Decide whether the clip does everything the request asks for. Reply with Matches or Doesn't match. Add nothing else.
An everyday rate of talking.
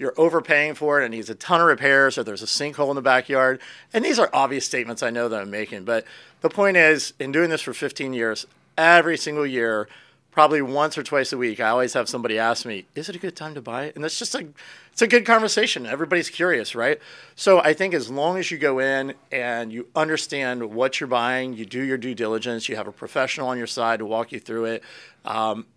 Doesn't match